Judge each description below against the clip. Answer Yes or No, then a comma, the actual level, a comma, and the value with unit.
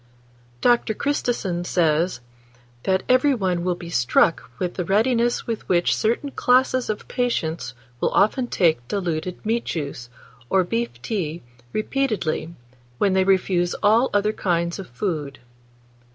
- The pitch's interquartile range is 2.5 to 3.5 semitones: No, average, 5.2 semitones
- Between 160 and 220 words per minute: No, slow, 135 wpm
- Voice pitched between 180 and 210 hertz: Yes, high, 190 Hz